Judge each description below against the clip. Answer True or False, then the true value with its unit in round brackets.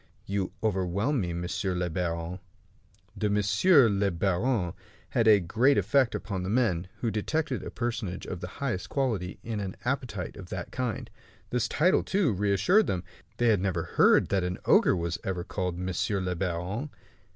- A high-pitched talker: False (100 Hz)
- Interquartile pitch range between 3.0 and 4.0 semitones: False (4.8 semitones)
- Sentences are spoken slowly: False (170 wpm)